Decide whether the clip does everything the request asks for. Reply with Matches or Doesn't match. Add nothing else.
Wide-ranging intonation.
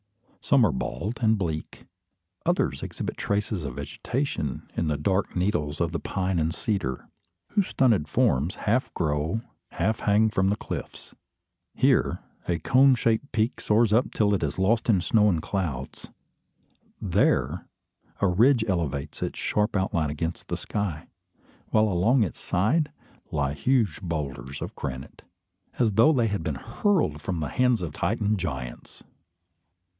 Matches